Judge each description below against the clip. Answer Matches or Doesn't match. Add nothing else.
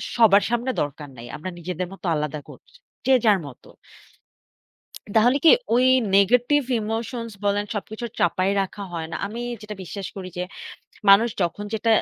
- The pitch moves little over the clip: Doesn't match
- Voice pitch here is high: Matches